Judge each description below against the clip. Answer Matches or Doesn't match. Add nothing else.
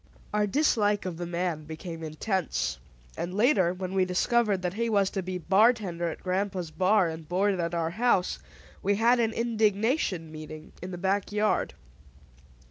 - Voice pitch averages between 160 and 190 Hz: Matches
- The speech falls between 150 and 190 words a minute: Matches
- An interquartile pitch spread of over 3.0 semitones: Matches